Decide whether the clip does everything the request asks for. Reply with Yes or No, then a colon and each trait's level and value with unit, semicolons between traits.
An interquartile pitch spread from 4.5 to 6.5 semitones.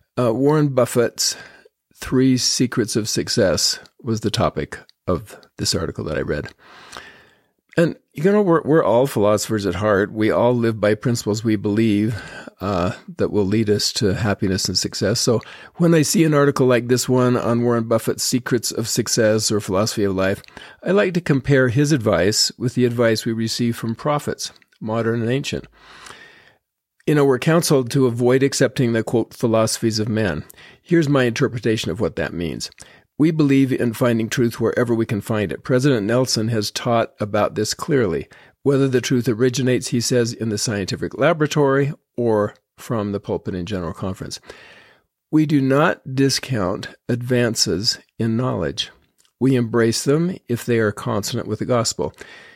No: average, 3.7 semitones